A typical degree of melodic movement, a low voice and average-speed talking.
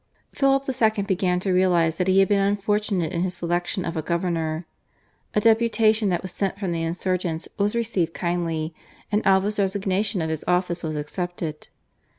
No: average, 3.1 semitones; medium, 185 Hz; average, 170 wpm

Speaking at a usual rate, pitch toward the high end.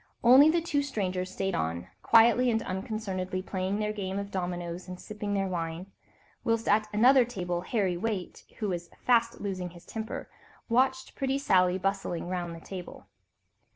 Yes: average, 160 wpm; high, 195 Hz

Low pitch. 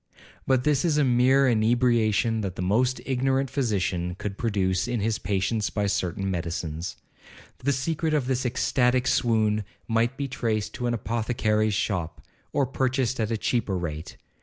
Yes: low, 115 Hz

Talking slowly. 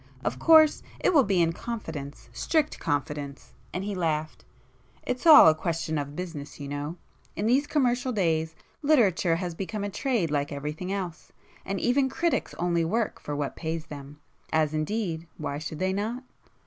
No: average, 165 wpm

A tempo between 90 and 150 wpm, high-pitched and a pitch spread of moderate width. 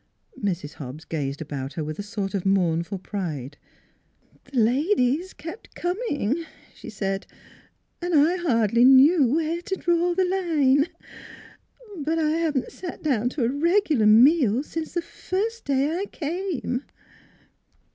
No: average, 145 wpm; very high, 280 Hz; wide, 8.9 semitones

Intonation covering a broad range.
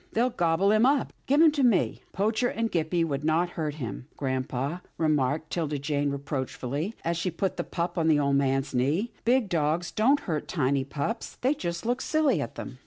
Yes: wide, 7.2 semitones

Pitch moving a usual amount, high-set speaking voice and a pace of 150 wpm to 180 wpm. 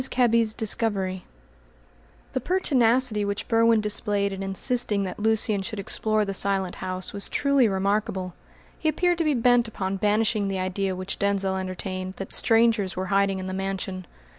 Yes: average, 3.1 semitones; high, 200 Hz; average, 160 wpm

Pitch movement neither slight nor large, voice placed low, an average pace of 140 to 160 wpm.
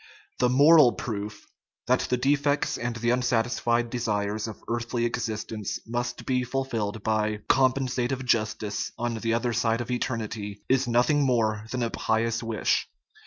No: narrow, 2.2 semitones; low, 120 Hz; average, 155 wpm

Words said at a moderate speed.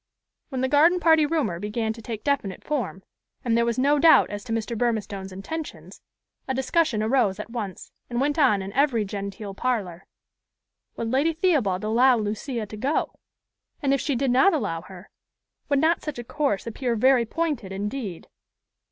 Yes: average, 175 wpm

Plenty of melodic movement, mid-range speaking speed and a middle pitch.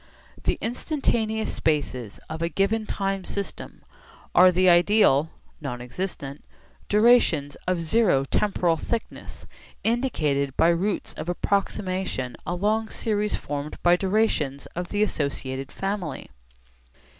No: wide, 6.2 semitones; slow, 110 wpm; medium, 180 Hz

